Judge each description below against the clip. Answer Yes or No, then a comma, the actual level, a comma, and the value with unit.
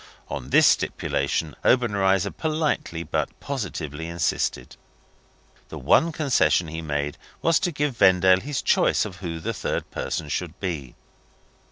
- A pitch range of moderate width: No, wide, 8.3 semitones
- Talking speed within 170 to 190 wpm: No, slow, 135 wpm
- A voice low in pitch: Yes, very low, 95 Hz